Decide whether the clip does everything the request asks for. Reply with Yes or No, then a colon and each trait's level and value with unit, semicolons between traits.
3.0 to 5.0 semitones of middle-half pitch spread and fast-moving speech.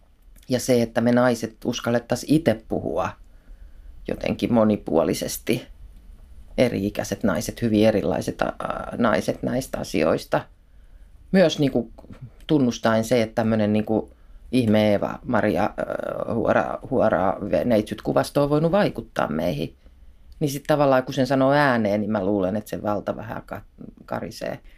No: average, 3.9 semitones; average, 120 wpm